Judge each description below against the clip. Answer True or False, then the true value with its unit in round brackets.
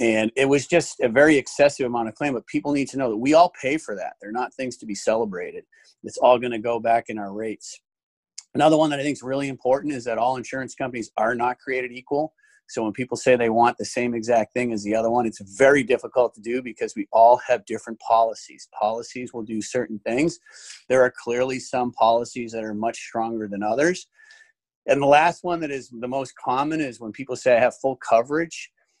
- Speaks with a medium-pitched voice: False (125 Hz)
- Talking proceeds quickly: True (230 wpm)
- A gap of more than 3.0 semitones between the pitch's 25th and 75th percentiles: True (3.6 semitones)